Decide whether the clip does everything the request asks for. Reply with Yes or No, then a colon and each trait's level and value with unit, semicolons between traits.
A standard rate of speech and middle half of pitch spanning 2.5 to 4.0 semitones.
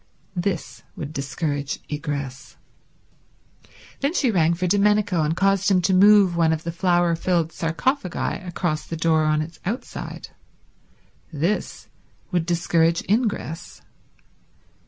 No: slow, 120 wpm; average, 3.5 semitones